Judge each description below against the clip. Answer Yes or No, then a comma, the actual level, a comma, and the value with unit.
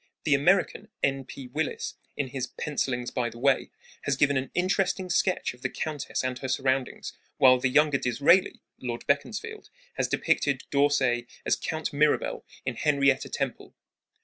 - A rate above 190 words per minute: No, average, 155 wpm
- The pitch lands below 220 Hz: Yes, medium, 140 Hz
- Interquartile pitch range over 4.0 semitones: No, average, 2.9 semitones